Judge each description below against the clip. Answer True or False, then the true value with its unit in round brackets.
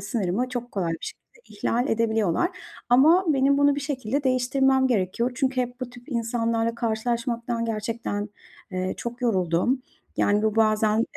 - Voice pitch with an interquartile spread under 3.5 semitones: True (2.9 semitones)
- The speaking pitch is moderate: False (235 Hz)